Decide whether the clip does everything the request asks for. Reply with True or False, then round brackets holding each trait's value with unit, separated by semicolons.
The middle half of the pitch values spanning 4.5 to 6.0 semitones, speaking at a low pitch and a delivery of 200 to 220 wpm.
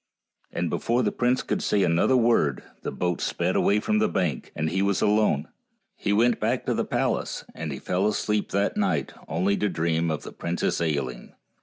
True (5.1 semitones; 100 Hz; 205 wpm)